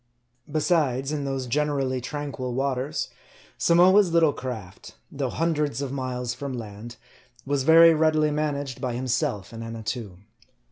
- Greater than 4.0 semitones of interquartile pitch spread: No, average, 3.4 semitones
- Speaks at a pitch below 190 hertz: Yes, low, 135 Hz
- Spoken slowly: Yes, slow, 130 wpm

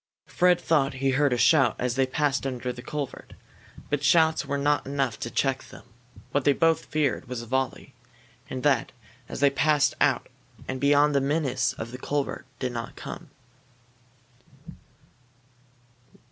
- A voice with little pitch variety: Yes, narrow, 2.3 semitones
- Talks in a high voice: No, low, 135 Hz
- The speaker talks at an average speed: Yes, average, 160 wpm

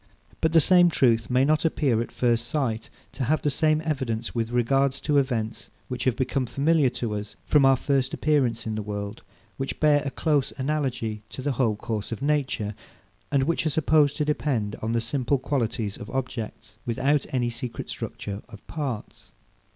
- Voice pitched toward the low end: Yes, low, 130 Hz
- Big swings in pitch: No, average, 4.2 semitones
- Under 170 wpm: No, average, 185 wpm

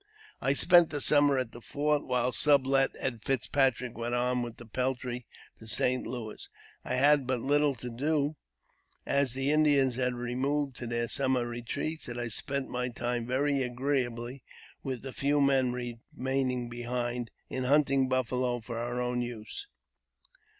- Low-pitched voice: Yes, low, 125 Hz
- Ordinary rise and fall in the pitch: No, narrow, 2.3 semitones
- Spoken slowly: No, average, 155 wpm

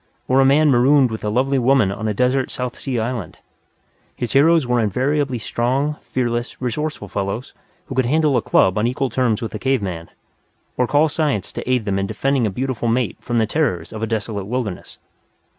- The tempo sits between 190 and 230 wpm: Yes, average, 200 wpm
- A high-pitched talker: No, low, 125 Hz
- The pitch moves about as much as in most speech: Yes, average, 3.6 semitones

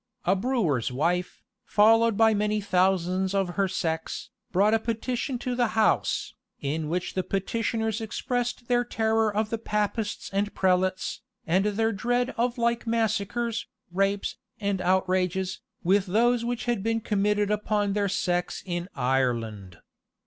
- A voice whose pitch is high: Yes, high, 205 Hz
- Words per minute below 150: Yes, average, 140 wpm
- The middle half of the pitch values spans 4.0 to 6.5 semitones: No, average, 3.6 semitones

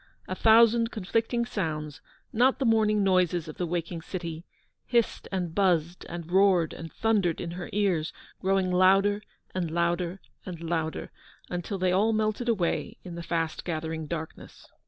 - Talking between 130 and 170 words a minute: Yes, average, 160 wpm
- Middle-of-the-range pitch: Yes, medium, 180 Hz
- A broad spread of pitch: No, average, 3.5 semitones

